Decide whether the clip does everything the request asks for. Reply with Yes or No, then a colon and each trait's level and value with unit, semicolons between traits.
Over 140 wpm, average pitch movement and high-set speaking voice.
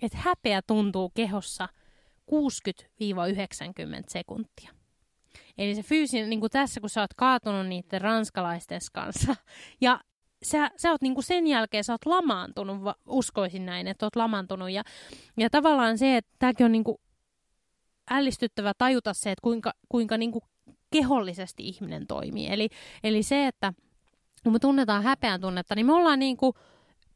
Yes: average, 150 wpm; average, 4.5 semitones; high, 225 Hz